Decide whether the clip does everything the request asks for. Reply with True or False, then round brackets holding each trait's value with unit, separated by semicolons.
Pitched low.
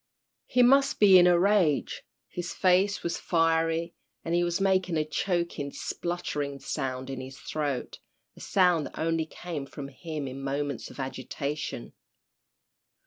False (165 Hz)